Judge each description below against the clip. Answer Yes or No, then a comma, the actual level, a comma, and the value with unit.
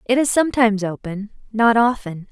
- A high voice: Yes, high, 220 Hz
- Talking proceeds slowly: Yes, slow, 130 wpm